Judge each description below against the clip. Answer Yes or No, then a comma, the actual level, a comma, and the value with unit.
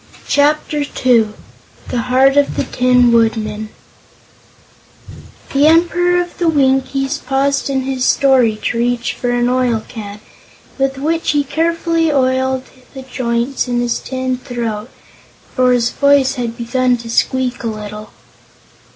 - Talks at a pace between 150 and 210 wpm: No, slow, 135 wpm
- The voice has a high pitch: Yes, very high, 255 Hz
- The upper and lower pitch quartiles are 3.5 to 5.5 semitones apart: No, average, 2.7 semitones